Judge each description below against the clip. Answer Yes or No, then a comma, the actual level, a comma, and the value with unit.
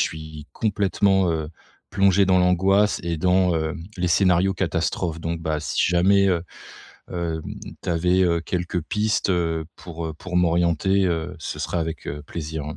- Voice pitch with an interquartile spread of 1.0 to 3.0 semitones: Yes, narrow, 2.5 semitones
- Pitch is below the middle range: Yes, very low, 85 Hz